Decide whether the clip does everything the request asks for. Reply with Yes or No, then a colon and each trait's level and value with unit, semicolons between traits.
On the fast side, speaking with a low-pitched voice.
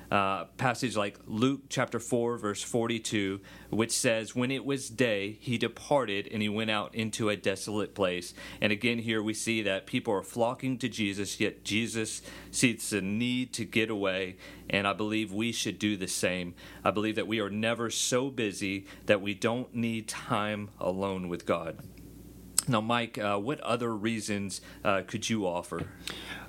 No: average, 170 wpm; low, 110 Hz